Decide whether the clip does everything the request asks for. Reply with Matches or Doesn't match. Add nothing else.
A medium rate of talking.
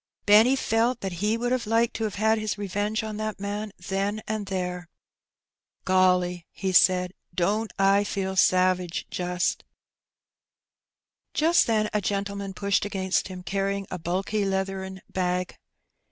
Matches